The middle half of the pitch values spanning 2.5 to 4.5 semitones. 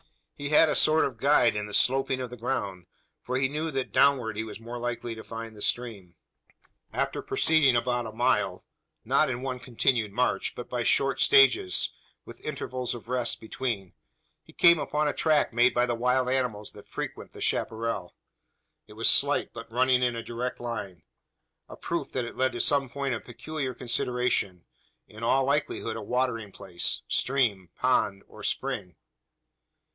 Yes: average, 2.9 semitones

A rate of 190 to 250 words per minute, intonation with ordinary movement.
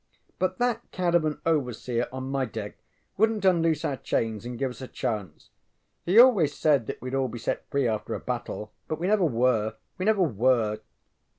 No: average, 195 wpm; wide, 6.6 semitones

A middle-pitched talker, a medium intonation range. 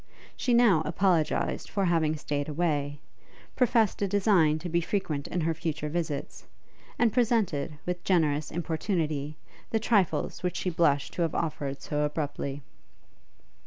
Yes: medium, 165 Hz; average, 4.2 semitones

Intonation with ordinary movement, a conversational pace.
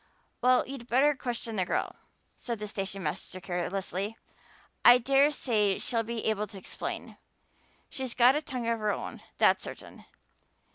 Yes: average, 4.0 semitones; average, 155 wpm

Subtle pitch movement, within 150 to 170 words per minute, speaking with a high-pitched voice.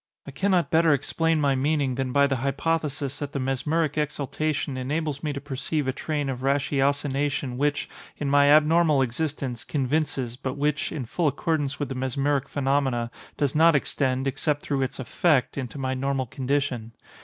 No: narrow, 2.1 semitones; average, 165 wpm; medium, 140 Hz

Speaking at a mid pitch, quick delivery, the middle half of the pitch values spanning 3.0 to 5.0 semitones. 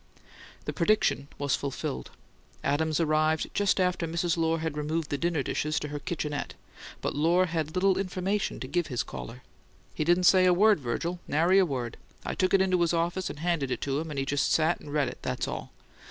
Yes: medium, 165 Hz; fast, 210 wpm; average, 3.5 semitones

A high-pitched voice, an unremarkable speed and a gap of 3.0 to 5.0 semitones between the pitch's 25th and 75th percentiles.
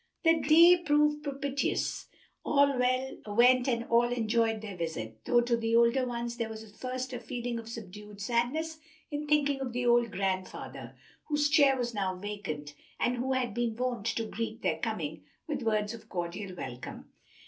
Yes: high, 235 Hz; average, 170 wpm; average, 3.9 semitones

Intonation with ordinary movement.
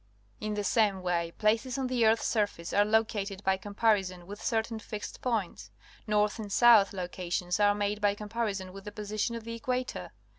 No: narrow, 2.3 semitones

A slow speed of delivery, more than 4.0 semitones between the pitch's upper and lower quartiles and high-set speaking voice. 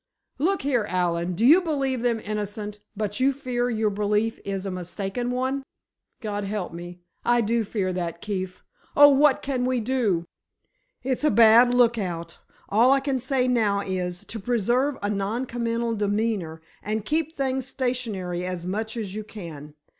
No: average, 160 wpm; average, 4.5 semitones; high, 220 Hz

